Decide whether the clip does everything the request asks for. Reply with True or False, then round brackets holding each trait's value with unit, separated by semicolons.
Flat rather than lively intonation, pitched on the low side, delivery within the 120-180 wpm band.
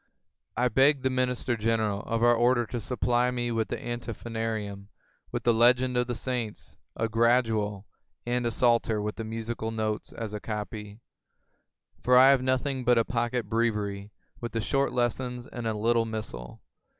True (2.0 semitones; 115 Hz; 170 wpm)